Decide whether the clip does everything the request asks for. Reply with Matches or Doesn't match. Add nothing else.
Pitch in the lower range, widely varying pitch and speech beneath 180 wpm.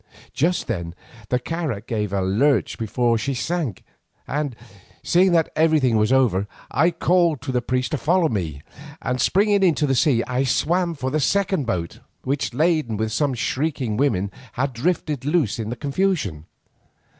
Matches